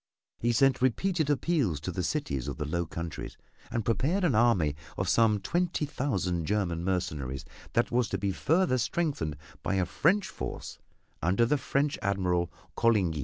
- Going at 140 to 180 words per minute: Yes, average, 165 wpm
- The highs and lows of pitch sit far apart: Yes, wide, 8.2 semitones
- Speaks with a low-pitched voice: Yes, low, 110 Hz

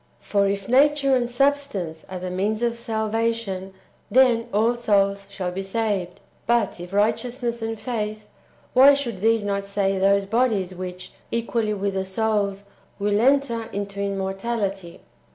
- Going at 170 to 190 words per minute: No, average, 145 wpm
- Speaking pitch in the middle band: No, high, 210 Hz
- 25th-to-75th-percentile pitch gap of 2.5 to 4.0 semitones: Yes, average, 3.2 semitones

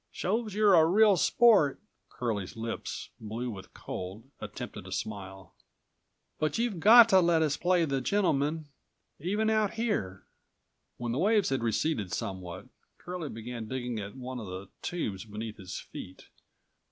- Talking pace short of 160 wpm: Yes, average, 150 wpm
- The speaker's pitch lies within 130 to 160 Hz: Yes, low, 135 Hz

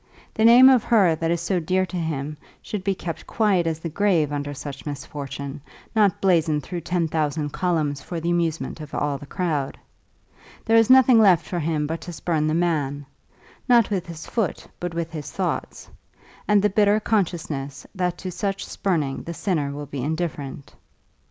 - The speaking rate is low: No, average, 185 wpm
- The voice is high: No, medium, 165 Hz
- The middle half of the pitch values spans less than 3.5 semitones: No, average, 4.2 semitones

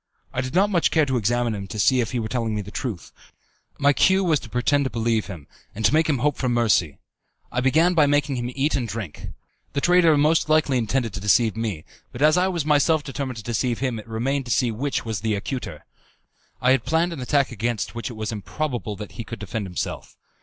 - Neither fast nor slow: No, fast, 240 wpm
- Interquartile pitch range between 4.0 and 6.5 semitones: Yes, average, 4.7 semitones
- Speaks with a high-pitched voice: No, low, 125 Hz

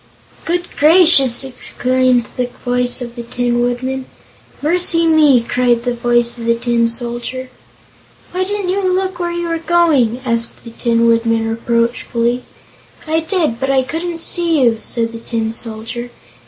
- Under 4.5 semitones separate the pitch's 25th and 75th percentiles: No, wide, 5.6 semitones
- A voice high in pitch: Yes, high, 245 Hz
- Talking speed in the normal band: Yes, average, 155 wpm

